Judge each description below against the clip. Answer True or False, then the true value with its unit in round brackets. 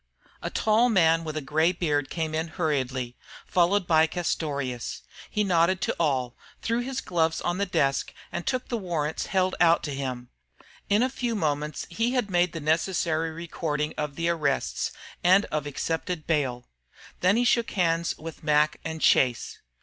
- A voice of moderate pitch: True (165 Hz)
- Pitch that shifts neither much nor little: True (3.6 semitones)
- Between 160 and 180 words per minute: True (170 wpm)